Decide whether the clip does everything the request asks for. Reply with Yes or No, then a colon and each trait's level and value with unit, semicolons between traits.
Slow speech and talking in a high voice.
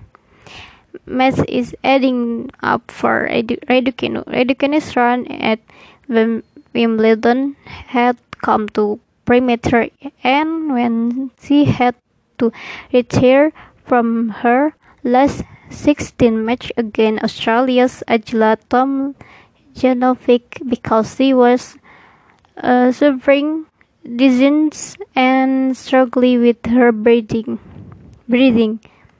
Yes: slow, 80 wpm; very high, 250 Hz